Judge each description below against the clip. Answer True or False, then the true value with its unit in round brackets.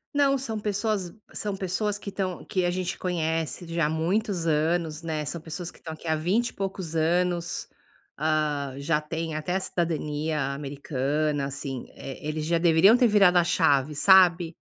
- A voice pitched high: False (165 Hz)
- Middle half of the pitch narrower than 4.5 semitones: True (3.4 semitones)